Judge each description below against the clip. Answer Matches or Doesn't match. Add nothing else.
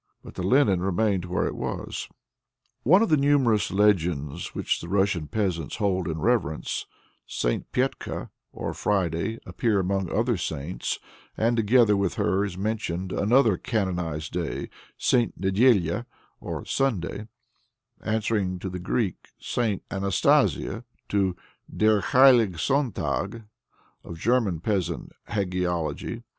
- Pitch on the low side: Matches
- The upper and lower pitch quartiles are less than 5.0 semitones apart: Matches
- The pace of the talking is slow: Matches